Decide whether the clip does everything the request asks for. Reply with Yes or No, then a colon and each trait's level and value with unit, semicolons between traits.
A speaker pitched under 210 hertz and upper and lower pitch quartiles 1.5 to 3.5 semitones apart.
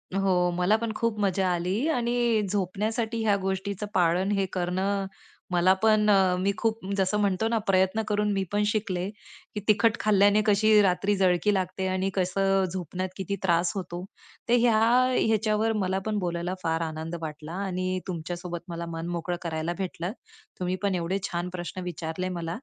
Yes: high, 190 Hz; average, 2.8 semitones